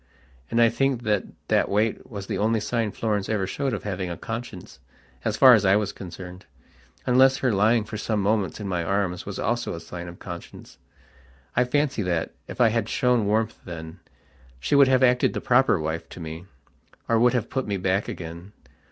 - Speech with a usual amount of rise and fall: Yes, average, 4.4 semitones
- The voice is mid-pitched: No, low, 105 Hz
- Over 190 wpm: Yes, average, 200 wpm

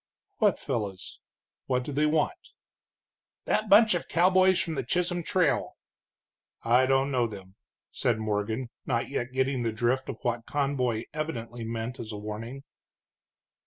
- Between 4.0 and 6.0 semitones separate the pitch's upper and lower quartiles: Yes, average, 4.8 semitones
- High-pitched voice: No, low, 125 Hz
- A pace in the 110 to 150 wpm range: Yes, average, 145 wpm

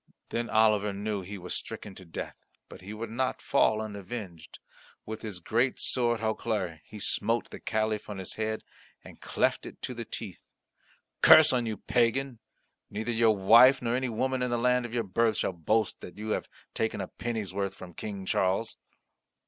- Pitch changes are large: No, average, 2.9 semitones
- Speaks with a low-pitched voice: Yes, low, 110 Hz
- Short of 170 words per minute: No, average, 185 wpm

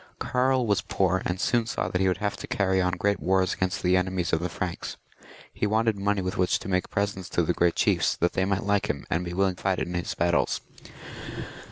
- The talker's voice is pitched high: No, very low, 95 Hz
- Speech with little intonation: Yes, narrow, 2.2 semitones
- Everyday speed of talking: No, fast, 235 wpm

